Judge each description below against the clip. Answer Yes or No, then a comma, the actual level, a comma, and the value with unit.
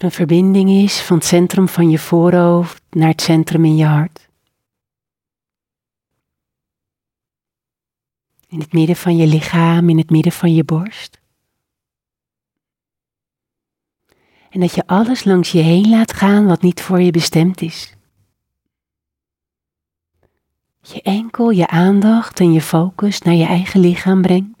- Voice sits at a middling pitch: Yes, medium, 170 Hz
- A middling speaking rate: No, slow, 130 wpm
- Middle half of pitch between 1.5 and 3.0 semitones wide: Yes, narrow, 2.6 semitones